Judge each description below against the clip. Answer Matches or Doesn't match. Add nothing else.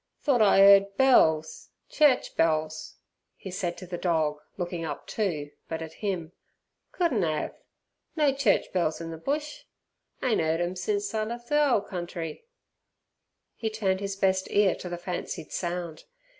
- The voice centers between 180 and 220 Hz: Matches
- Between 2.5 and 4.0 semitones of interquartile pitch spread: Doesn't match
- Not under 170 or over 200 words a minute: Doesn't match